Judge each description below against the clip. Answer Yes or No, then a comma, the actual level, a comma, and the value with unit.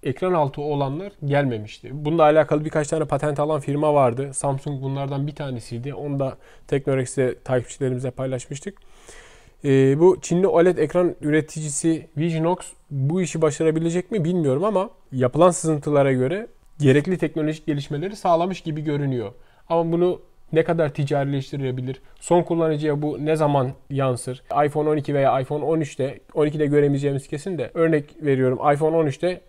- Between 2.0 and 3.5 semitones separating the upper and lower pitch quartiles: Yes, average, 2.9 semitones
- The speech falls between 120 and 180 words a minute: Yes, average, 135 wpm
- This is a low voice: No, medium, 150 Hz